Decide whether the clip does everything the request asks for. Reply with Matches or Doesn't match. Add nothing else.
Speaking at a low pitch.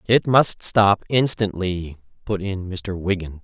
Matches